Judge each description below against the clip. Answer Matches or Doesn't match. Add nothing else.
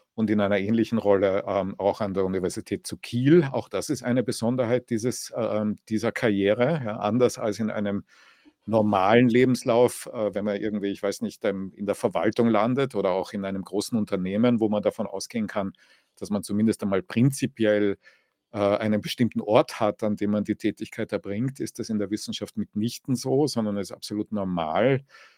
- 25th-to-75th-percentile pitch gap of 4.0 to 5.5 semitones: Doesn't match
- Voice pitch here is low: Matches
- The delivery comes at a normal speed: Matches